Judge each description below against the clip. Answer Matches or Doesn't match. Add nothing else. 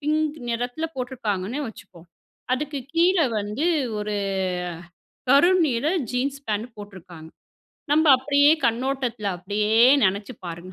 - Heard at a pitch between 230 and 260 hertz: Matches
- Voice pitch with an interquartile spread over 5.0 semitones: Matches